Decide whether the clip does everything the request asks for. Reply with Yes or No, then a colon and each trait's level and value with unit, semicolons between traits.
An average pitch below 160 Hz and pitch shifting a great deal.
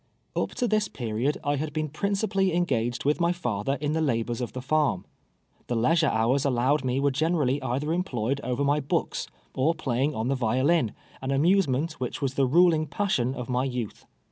No: medium, 140 Hz; average, 4.2 semitones